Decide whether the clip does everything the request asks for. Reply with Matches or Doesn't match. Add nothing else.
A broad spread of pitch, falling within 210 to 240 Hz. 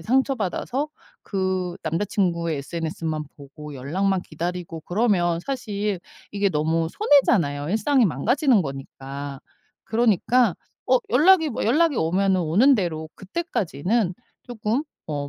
Doesn't match